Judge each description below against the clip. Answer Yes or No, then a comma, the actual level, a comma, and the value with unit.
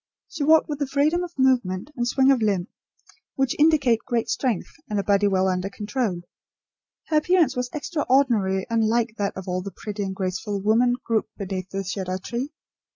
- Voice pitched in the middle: No, high, 225 Hz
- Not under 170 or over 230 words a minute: Yes, average, 180 wpm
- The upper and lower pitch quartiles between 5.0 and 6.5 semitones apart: Yes, wide, 5.6 semitones